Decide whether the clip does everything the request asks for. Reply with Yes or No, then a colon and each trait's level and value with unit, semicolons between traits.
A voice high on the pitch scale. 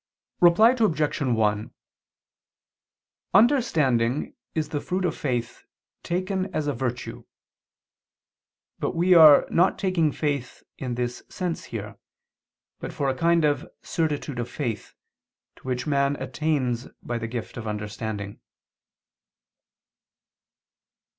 No: medium, 140 Hz